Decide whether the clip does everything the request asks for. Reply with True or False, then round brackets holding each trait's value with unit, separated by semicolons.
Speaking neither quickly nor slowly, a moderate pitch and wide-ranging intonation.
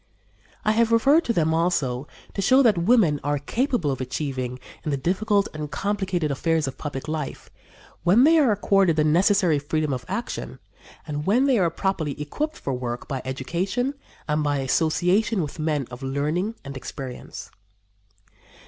True (165 wpm; 160 Hz; 6.3 semitones)